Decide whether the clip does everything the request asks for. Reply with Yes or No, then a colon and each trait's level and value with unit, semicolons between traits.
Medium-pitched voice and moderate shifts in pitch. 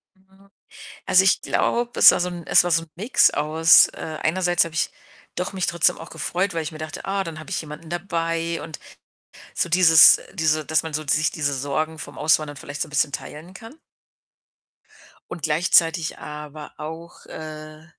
No: medium, 160 Hz; narrow, 2.3 semitones